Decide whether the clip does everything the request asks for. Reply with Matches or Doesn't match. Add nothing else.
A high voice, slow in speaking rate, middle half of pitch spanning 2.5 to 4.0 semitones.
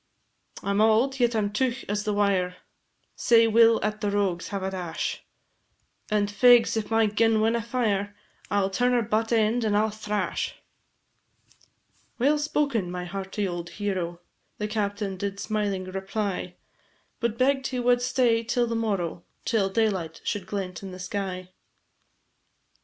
Doesn't match